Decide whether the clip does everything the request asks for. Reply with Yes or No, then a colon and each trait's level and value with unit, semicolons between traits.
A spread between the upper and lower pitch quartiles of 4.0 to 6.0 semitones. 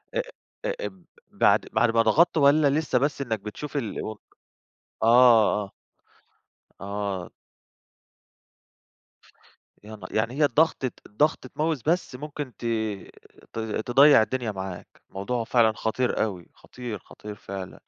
Yes: average, 5.0 semitones